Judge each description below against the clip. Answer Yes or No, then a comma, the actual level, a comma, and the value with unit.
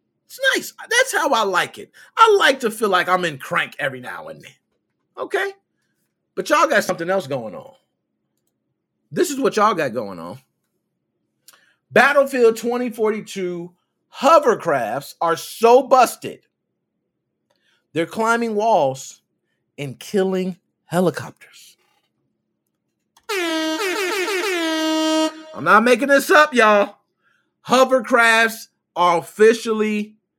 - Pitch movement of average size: No, wide, 8.7 semitones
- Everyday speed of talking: No, slow, 110 wpm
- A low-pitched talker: No, high, 230 Hz